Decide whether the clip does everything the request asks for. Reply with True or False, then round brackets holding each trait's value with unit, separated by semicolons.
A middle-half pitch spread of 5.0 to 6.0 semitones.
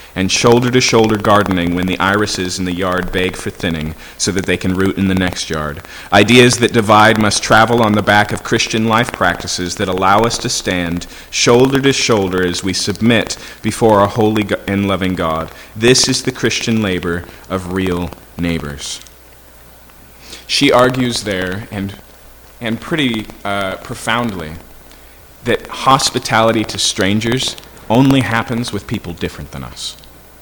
False (4.4 semitones)